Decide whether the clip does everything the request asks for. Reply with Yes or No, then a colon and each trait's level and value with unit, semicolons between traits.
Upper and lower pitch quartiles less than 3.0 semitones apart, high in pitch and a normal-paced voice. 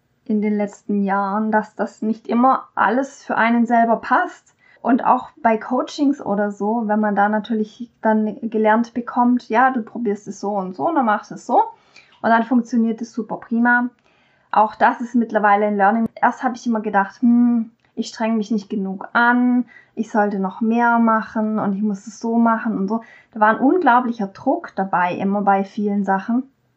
No: narrow, 2.6 semitones; high, 225 Hz; fast, 195 wpm